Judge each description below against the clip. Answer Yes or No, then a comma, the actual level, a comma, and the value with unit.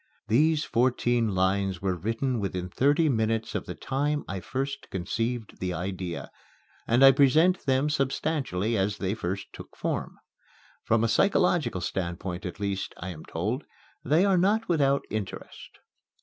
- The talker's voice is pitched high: No, low, 115 Hz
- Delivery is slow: No, average, 150 wpm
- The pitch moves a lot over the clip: Yes, wide, 6.6 semitones